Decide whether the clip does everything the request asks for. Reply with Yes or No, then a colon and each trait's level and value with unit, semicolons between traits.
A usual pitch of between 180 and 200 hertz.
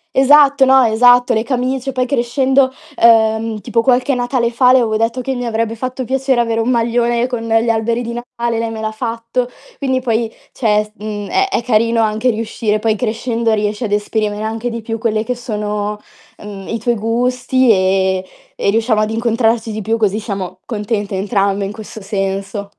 No: high, 230 Hz